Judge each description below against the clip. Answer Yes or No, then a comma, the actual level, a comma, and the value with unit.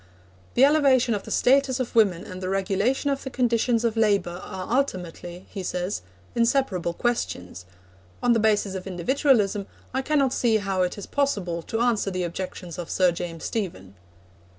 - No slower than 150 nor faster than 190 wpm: Yes, average, 170 wpm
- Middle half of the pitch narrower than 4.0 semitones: No, average, 5.2 semitones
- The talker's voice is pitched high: Yes, high, 205 Hz